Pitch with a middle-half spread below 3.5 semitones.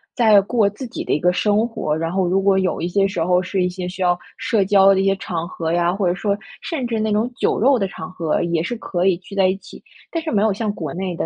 Yes: average, 2.8 semitones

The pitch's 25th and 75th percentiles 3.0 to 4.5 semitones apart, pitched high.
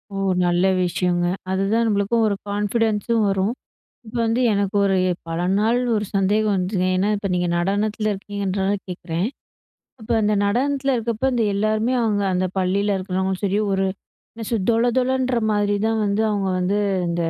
No: narrow, 2.6 semitones; high, 205 Hz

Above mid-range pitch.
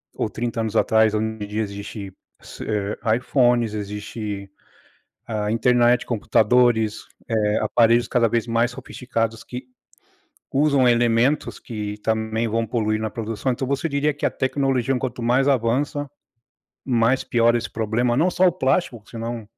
No: low, 115 Hz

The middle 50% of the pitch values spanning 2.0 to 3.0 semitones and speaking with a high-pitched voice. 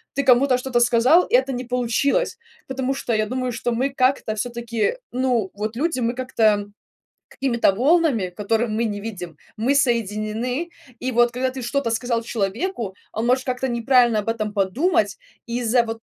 Yes: average, 2.7 semitones; high, 240 Hz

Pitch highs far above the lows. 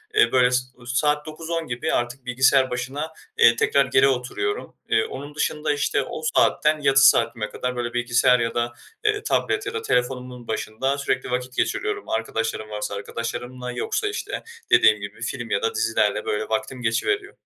No: average, 4.0 semitones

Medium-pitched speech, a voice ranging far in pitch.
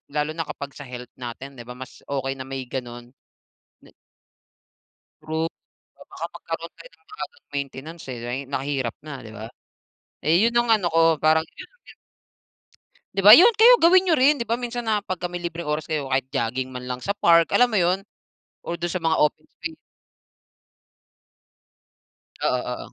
Yes: medium, 155 Hz; wide, 8.0 semitones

